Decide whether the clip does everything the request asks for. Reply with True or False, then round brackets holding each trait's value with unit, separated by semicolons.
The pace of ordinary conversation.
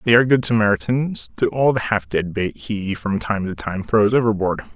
False (215 wpm)